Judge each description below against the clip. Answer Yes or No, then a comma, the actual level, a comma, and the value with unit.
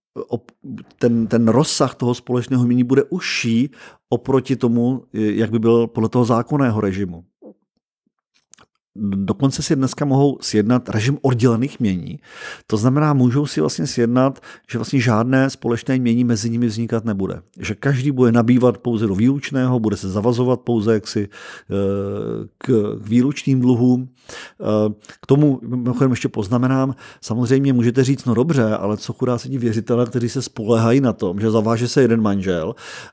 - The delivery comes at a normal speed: Yes, average, 145 wpm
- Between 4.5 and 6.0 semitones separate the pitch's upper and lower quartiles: No, average, 2.8 semitones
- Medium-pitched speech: No, low, 120 Hz